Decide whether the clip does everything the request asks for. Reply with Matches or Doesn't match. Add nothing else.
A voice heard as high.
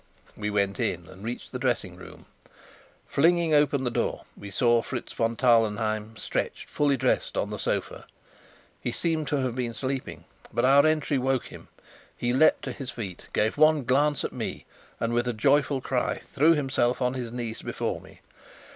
Doesn't match